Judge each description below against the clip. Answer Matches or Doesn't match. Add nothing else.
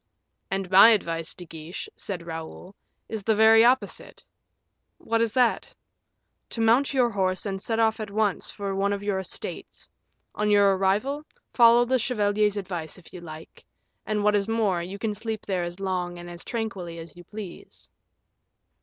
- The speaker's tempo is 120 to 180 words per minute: Matches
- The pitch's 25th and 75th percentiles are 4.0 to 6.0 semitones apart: Doesn't match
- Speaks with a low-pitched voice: Doesn't match